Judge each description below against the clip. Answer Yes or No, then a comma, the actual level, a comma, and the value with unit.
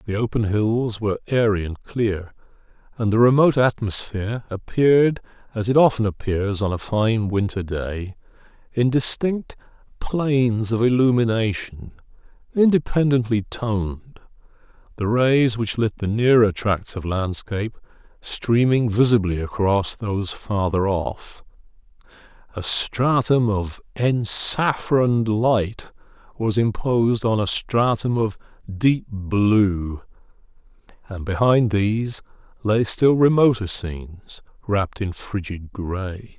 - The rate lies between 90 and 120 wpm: Yes, slow, 110 wpm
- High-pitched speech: No, low, 110 Hz